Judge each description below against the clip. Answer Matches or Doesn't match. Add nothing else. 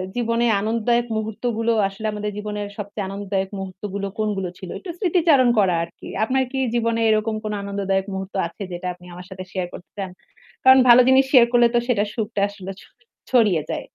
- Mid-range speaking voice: Doesn't match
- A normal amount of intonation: Matches